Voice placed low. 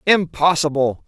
No: medium, 160 Hz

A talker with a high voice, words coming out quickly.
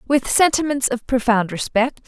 No: very high, 250 Hz; average, 145 wpm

